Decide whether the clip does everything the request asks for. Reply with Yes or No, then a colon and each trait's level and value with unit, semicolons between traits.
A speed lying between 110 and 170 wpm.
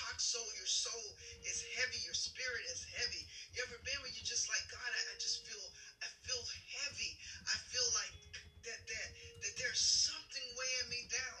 No: average, 185 wpm